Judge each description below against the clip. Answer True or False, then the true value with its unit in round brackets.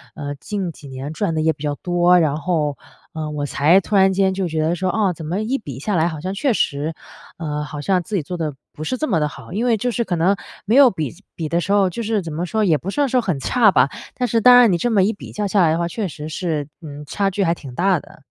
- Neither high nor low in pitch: True (175 Hz)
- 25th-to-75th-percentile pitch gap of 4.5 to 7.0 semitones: True (4.8 semitones)